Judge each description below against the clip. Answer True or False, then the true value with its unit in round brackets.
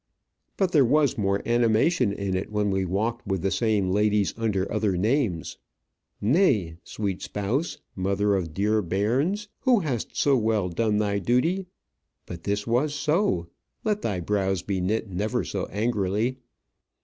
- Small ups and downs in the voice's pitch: False (4.2 semitones)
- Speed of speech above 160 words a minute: False (150 wpm)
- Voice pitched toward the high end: False (105 Hz)